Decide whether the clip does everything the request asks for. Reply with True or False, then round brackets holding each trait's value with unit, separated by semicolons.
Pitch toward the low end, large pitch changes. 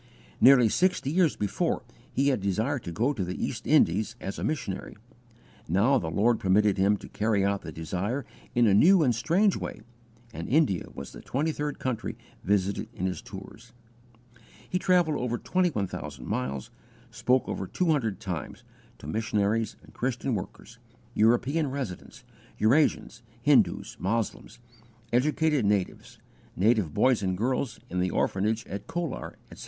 True (115 Hz; 6.1 semitones)